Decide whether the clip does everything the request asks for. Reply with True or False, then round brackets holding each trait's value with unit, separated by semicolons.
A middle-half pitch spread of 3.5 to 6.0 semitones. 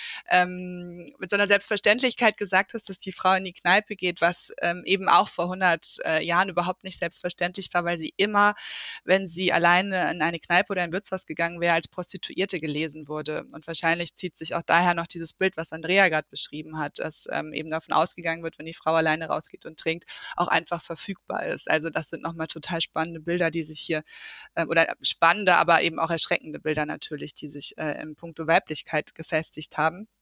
False (2.7 semitones)